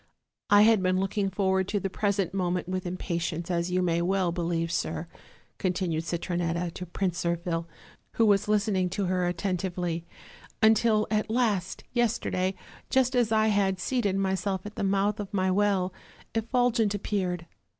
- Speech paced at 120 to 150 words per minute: No, average, 160 wpm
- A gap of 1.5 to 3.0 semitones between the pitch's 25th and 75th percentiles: Yes, average, 2.7 semitones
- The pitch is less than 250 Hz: Yes, high, 190 Hz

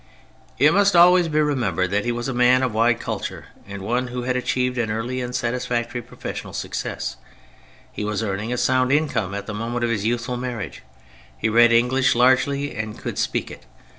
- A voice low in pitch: Yes, low, 120 Hz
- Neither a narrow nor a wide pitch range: No, narrow, 2.3 semitones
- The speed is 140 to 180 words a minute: No, average, 195 wpm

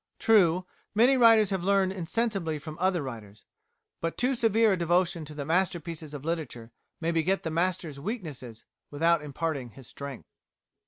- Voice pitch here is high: No, medium, 170 Hz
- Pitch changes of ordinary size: Yes, average, 4.4 semitones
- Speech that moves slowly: No, average, 155 wpm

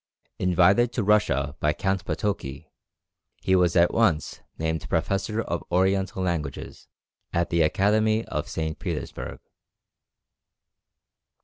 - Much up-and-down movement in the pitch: No, average, 4.1 semitones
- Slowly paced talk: Yes, slow, 110 wpm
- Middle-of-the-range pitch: No, very low, 90 Hz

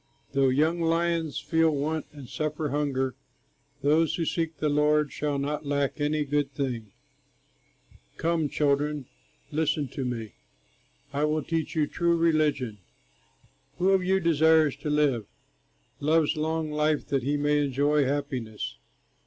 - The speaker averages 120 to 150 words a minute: Yes, slow, 135 wpm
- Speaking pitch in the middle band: Yes, medium, 150 Hz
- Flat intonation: Yes, narrow, 2.1 semitones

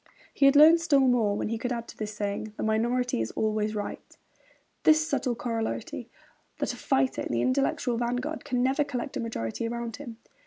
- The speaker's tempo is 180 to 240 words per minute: Yes, average, 195 wpm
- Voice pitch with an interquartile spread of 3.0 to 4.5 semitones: Yes, average, 3.5 semitones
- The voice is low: No, high, 235 Hz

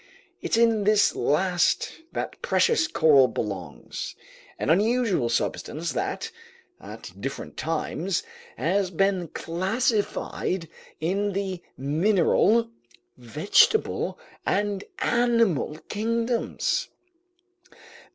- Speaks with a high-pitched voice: Yes, high, 195 Hz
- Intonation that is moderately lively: No, wide, 5.8 semitones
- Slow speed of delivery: Yes, slow, 85 wpm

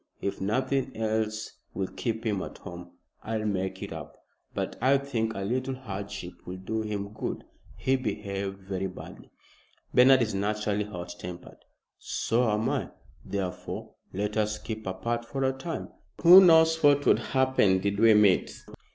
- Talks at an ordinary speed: Yes, average, 160 wpm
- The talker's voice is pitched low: Yes, low, 110 Hz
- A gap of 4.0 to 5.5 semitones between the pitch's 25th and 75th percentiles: Yes, average, 4.7 semitones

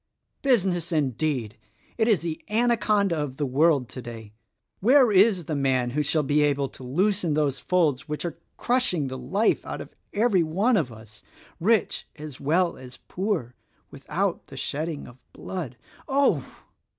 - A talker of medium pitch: Yes, medium, 155 Hz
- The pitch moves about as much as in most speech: No, wide, 6.7 semitones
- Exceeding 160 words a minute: No, average, 155 wpm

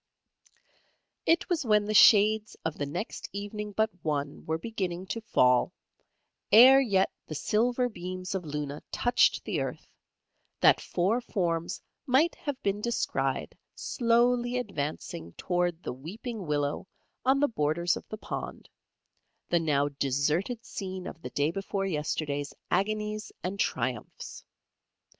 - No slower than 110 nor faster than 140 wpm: Yes, slow, 135 wpm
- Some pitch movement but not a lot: No, wide, 6.5 semitones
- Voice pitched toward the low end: No, high, 190 Hz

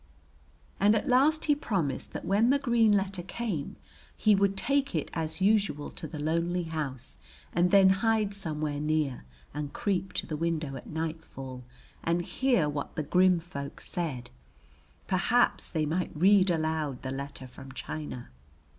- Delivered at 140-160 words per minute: Yes, average, 155 wpm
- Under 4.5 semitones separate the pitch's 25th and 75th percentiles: No, average, 5.0 semitones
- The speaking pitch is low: No, medium, 170 Hz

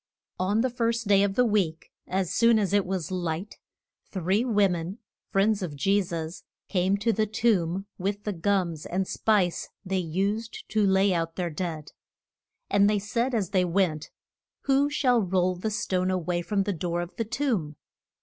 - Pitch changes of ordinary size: Yes, average, 3.2 semitones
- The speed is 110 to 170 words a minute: No, average, 180 wpm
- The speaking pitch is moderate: No, high, 195 Hz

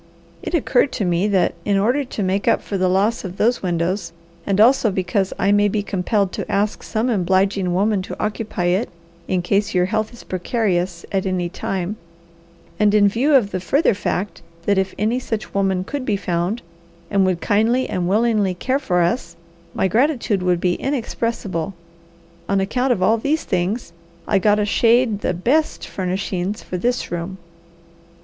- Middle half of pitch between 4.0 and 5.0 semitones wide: No, average, 3.3 semitones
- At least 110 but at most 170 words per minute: No, average, 180 wpm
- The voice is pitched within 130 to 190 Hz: No, high, 200 Hz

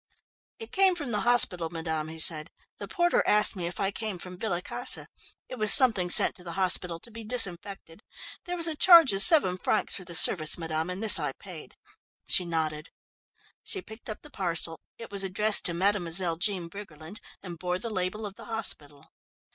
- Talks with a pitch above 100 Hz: Yes, high, 190 Hz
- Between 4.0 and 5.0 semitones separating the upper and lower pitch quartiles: Yes, average, 4.4 semitones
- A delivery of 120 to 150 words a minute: No, average, 195 wpm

